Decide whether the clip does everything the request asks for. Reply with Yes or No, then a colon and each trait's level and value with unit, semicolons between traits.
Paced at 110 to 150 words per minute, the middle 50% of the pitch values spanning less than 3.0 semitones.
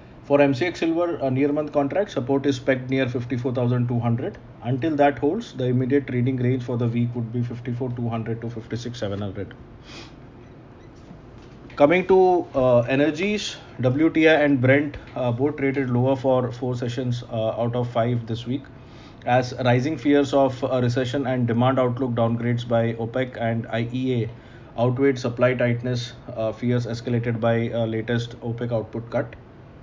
Yes: average, 145 wpm; narrow, 2.4 semitones